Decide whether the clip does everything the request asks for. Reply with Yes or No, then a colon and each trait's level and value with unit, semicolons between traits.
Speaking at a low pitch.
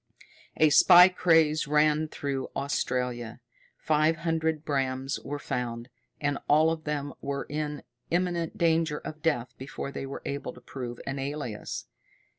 No: medium, 145 Hz